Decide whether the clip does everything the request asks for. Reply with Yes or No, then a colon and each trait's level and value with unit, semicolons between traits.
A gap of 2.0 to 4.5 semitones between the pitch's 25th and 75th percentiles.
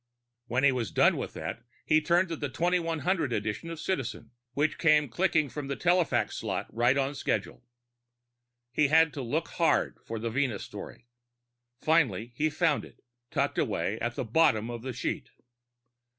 No: average, 5.3 semitones